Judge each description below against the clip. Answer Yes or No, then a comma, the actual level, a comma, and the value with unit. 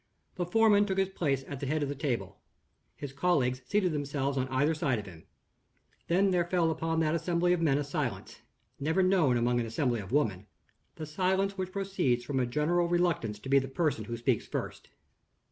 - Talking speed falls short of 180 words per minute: No, average, 200 wpm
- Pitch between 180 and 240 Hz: No, medium, 150 Hz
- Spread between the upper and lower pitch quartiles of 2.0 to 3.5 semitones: No, average, 5.3 semitones